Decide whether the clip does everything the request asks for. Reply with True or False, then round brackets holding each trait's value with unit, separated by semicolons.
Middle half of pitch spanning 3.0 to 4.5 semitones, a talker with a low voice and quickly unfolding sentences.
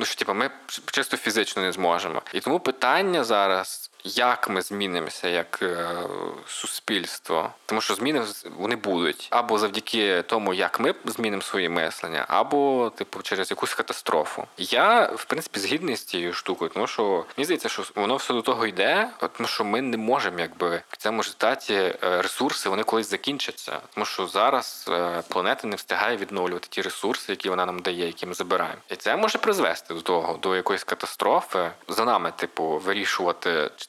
True (3.7 semitones; 95 Hz; 175 wpm)